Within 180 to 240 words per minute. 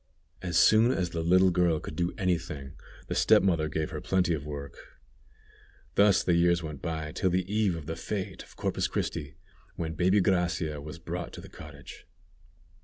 Yes: average, 185 wpm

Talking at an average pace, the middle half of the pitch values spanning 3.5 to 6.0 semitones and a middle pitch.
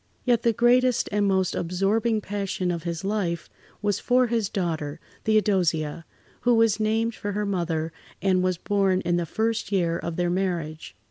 No: average, 170 wpm; average, 4.1 semitones; high, 195 Hz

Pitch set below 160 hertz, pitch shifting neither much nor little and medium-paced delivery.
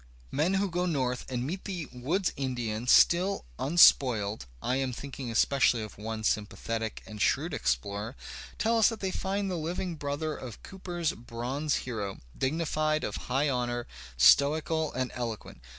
No: low, 135 Hz; wide, 6.2 semitones; average, 155 wpm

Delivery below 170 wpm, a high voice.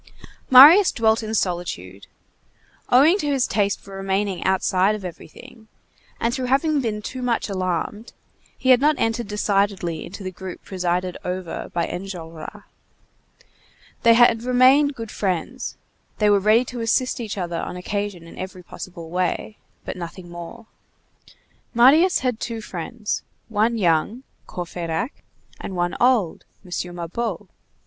Yes: average, 140 wpm; high, 205 Hz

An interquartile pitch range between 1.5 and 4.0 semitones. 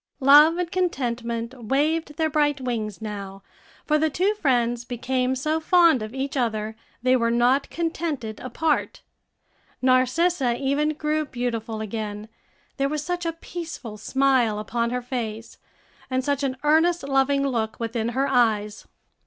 No: average, 4.6 semitones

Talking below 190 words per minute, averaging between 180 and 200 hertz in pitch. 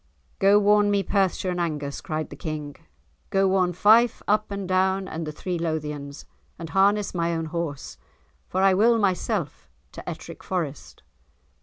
Yes: average, 160 wpm; medium, 185 Hz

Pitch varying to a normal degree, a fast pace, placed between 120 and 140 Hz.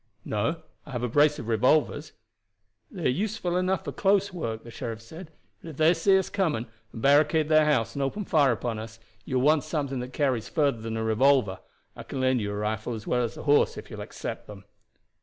No: wide, 5.7 semitones; fast, 230 wpm; low, 135 Hz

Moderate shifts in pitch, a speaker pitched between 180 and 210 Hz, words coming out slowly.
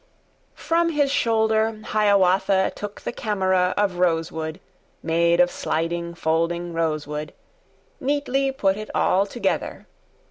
Yes: average, 4.6 semitones; high, 190 Hz; slow, 115 wpm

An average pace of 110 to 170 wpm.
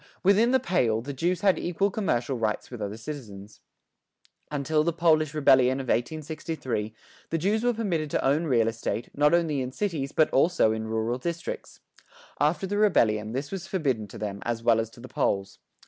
No: average, 185 wpm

